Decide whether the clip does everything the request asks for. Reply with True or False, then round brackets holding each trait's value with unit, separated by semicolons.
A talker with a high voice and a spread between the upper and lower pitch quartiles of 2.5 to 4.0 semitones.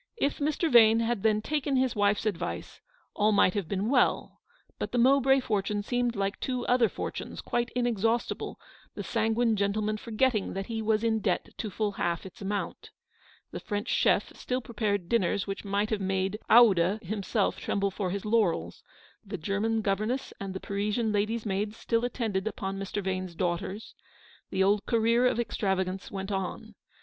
True (210 Hz; 2.9 semitones)